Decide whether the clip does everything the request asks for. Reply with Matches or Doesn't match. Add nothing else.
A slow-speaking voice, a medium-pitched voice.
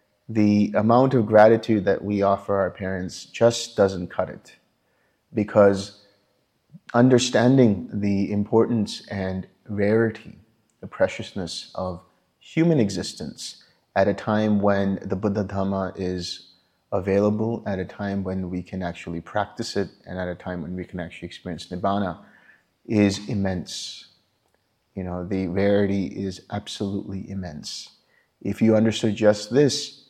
Doesn't match